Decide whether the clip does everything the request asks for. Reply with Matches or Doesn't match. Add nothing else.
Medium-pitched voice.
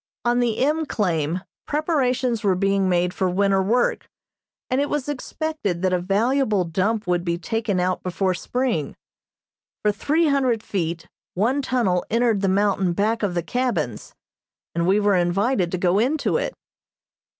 Doesn't match